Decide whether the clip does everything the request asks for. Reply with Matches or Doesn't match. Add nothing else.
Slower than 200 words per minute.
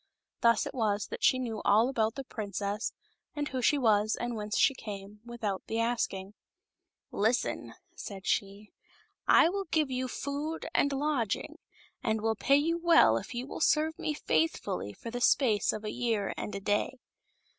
Matches